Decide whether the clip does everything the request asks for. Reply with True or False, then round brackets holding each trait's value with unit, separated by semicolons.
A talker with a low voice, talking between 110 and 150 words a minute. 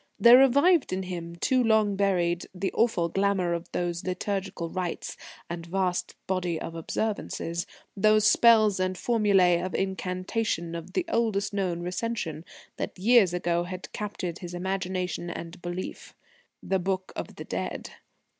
False (185 Hz; 145 wpm)